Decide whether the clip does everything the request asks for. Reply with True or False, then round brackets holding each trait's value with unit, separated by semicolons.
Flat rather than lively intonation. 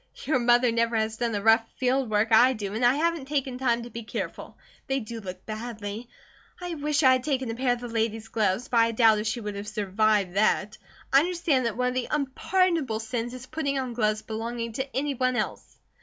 False (3.2 semitones)